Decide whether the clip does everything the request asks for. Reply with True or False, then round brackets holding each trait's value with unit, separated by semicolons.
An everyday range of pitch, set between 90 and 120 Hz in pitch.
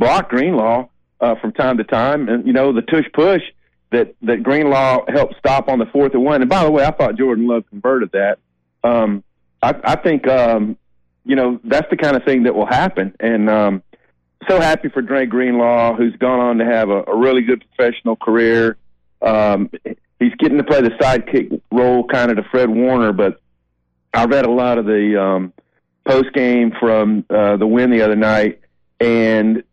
True (3.9 semitones; 115 Hz)